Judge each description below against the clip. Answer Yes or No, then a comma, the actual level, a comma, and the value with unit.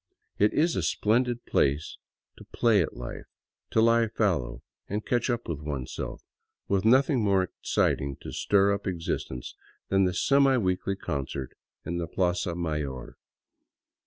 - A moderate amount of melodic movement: No, wide, 6.9 semitones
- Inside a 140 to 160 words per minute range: Yes, average, 145 wpm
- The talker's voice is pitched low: Yes, very low, 95 Hz